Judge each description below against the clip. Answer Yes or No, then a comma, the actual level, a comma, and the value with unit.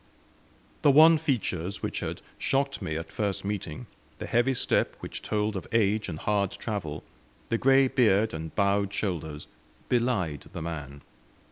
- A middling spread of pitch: No, wide, 6.3 semitones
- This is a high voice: No, low, 100 Hz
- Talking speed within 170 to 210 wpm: No, average, 150 wpm